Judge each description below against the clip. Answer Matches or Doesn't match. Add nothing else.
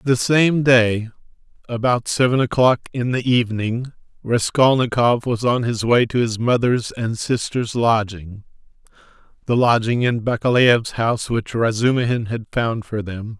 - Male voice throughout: Matches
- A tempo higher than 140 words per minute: Doesn't match